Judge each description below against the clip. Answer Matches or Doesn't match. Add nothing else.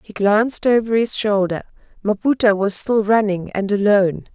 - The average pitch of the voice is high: Matches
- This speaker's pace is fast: Doesn't match